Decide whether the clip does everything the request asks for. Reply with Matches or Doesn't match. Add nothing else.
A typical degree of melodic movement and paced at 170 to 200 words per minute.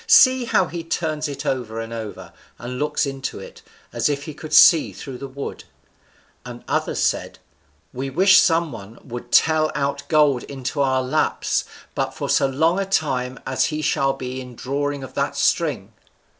Matches